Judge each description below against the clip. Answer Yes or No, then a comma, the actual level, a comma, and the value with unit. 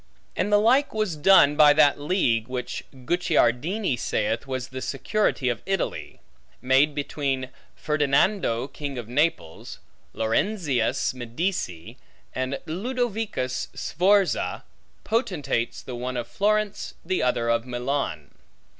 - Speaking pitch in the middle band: Yes, medium, 145 Hz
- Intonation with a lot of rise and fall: Yes, wide, 7.3 semitones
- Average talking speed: No, slow, 115 wpm